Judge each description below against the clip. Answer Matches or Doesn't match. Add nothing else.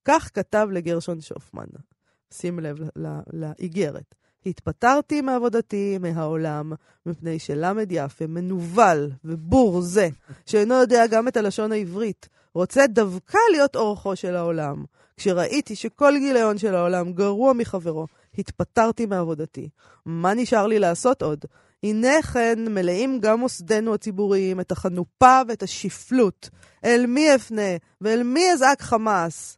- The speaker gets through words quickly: Doesn't match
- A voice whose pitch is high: Matches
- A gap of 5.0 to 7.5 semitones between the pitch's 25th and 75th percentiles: Matches